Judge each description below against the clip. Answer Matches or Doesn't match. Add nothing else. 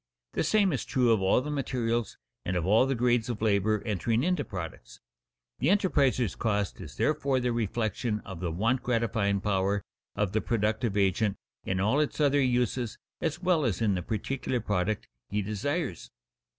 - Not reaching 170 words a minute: Doesn't match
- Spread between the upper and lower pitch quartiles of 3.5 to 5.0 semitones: Matches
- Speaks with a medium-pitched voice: Doesn't match